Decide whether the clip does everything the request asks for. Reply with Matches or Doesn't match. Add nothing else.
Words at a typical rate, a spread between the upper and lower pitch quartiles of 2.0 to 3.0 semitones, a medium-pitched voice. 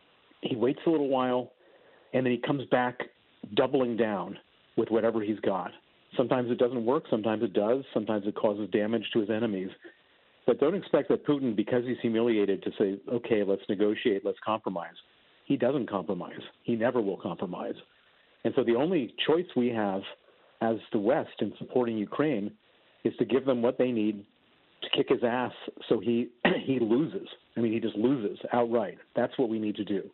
Doesn't match